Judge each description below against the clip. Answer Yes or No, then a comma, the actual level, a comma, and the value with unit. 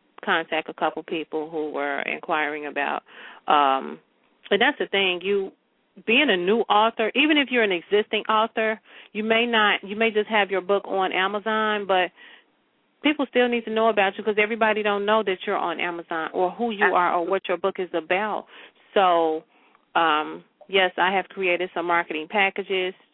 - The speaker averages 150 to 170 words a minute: No, average, 180 wpm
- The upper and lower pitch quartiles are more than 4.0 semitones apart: No, average, 3.7 semitones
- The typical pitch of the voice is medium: No, high, 195 Hz